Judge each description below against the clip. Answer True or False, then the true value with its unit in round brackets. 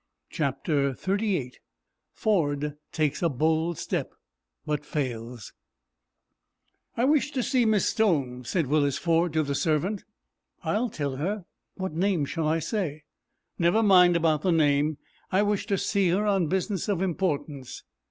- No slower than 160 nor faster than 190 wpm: False (140 wpm)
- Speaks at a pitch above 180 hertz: False (165 Hz)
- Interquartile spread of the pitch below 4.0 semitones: False (5.1 semitones)